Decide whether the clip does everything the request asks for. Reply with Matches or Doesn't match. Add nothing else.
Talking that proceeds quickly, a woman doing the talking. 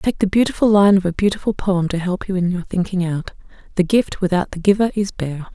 Matches